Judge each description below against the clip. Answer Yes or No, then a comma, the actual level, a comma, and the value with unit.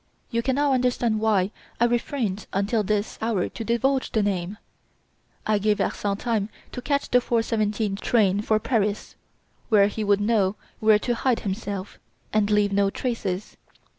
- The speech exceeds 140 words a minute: Yes, average, 160 wpm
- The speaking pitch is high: Yes, high, 215 Hz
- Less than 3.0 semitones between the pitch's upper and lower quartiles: Yes, narrow, 2.6 semitones